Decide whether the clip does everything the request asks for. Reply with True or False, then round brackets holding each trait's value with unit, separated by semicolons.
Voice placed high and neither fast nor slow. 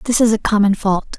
False (210 Hz; 255 wpm)